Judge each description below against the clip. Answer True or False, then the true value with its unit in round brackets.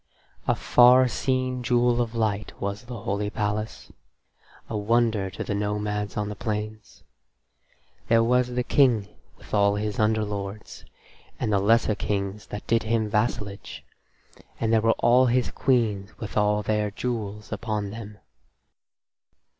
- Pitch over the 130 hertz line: False (110 Hz)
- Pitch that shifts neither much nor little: False (2.3 semitones)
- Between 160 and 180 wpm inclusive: False (140 wpm)